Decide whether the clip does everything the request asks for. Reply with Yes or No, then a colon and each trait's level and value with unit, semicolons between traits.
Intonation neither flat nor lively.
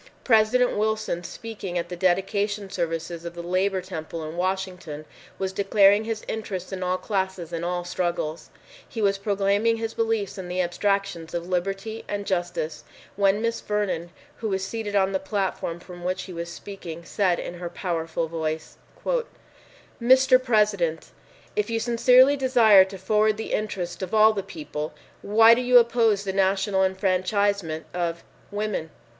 Yes: average, 3.5 semitones